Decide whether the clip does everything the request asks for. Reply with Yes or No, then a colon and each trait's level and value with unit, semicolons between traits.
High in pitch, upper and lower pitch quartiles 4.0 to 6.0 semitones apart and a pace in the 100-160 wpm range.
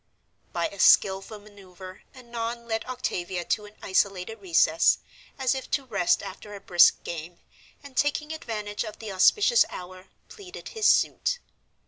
Yes: high, 210 Hz; wide, 5.4 semitones; average, 145 wpm